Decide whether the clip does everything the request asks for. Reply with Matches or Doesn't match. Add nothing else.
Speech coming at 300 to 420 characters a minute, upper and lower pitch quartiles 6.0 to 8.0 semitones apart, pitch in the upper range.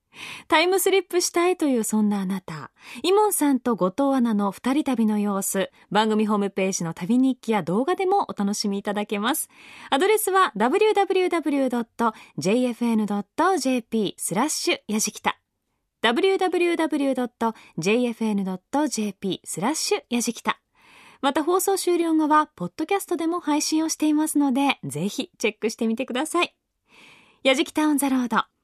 Doesn't match